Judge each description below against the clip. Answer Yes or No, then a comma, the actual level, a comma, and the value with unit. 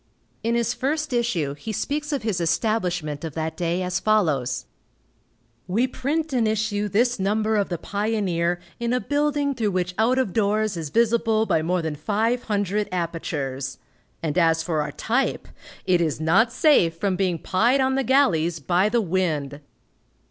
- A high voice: Yes, high, 200 Hz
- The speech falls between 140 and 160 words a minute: No, average, 170 wpm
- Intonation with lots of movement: Yes, wide, 5.9 semitones